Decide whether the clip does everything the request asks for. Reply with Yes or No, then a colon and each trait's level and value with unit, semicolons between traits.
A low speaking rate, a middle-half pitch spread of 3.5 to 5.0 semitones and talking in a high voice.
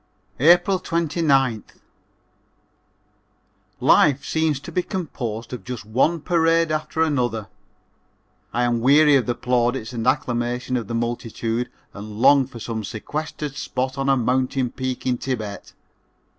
No: slow, 130 wpm; average, 4.1 semitones; low, 130 Hz